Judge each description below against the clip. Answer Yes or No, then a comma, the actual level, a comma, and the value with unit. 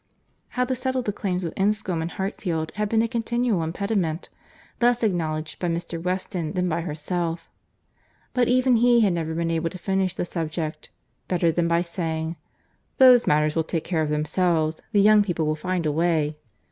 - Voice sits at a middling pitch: Yes, medium, 175 Hz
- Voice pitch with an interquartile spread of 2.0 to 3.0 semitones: No, average, 4.3 semitones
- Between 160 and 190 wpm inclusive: Yes, average, 170 wpm